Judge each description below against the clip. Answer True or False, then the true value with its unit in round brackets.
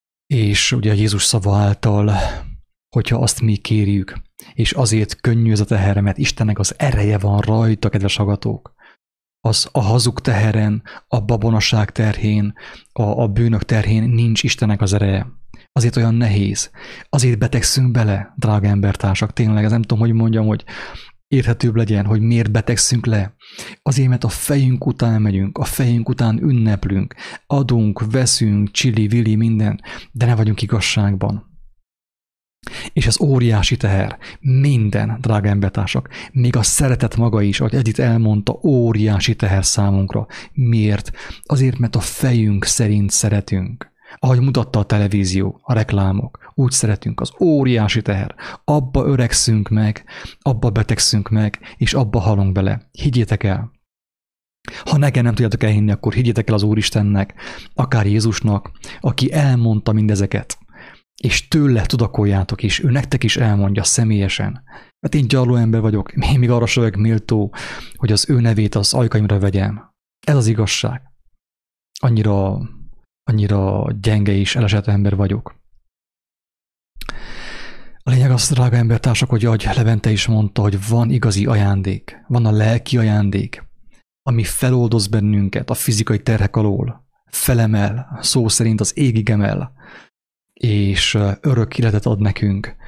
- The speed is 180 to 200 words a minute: False (140 wpm)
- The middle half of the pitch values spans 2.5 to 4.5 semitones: True (2.9 semitones)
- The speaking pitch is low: True (110 Hz)